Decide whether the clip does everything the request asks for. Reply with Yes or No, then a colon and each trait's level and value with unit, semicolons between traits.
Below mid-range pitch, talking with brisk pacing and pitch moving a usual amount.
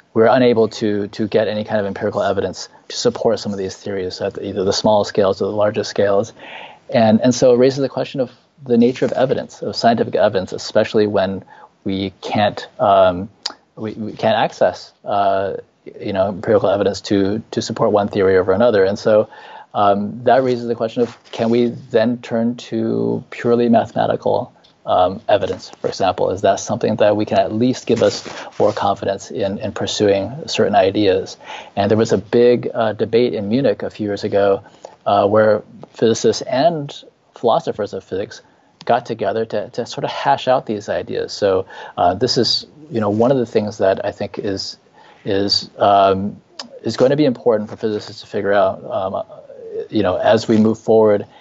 No: low, 110 Hz; average, 190 wpm; average, 3.0 semitones